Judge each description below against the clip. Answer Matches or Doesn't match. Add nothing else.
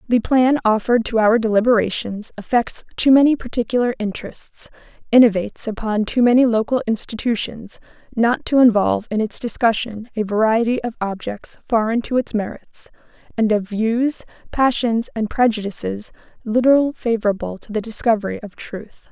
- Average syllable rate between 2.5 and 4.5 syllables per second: Doesn't match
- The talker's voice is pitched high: Matches